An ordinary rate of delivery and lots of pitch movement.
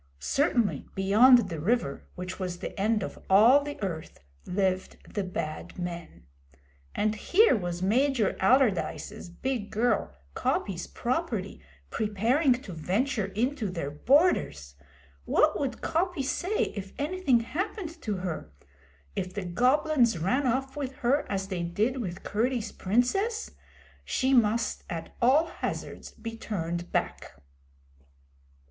No: slow, 130 wpm; wide, 6.4 semitones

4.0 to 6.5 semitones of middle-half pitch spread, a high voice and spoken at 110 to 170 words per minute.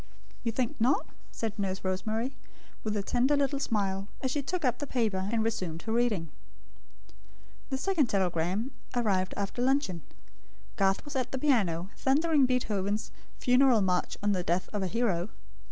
Yes: average, 5.3 semitones; high, 220 Hz; average, 160 wpm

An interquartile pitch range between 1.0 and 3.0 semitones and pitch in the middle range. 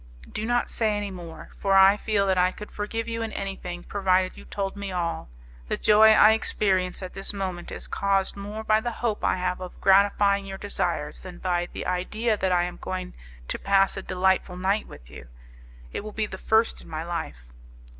No: narrow, 2.4 semitones; high, 195 Hz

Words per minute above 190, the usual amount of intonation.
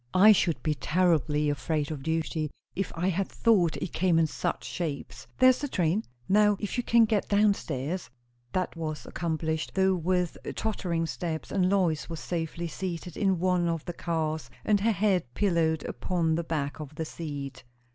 No: average, 175 wpm; average, 3.3 semitones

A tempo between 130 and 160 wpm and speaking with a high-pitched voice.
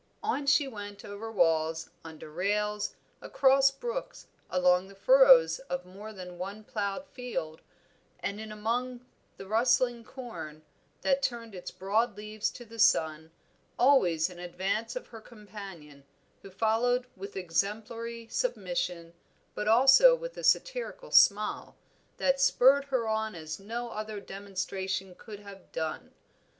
Yes: slow, 135 wpm; high, 210 Hz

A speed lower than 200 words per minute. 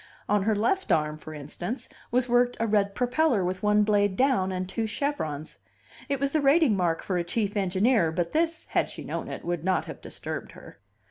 No: fast, 205 wpm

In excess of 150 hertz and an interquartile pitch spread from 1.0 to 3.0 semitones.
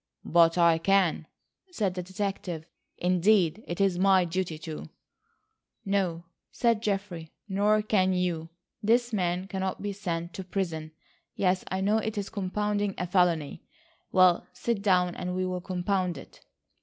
Yes: medium, 185 Hz; narrow, 2.5 semitones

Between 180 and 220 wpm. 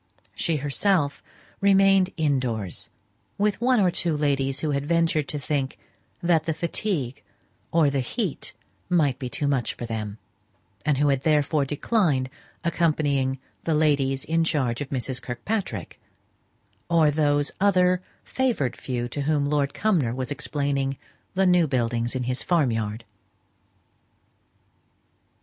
No: slow, 135 wpm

